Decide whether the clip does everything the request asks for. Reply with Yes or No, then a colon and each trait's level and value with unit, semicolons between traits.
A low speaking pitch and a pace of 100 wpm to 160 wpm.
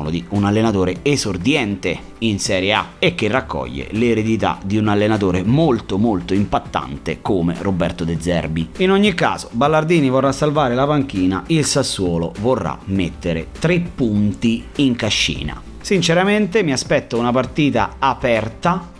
Yes: low, 110 Hz; average, 135 wpm